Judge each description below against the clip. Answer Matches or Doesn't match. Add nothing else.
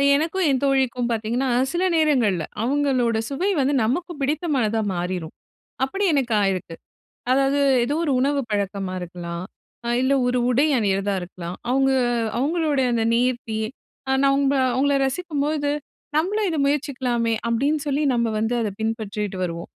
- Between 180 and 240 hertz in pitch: Doesn't match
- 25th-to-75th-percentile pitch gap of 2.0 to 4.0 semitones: Doesn't match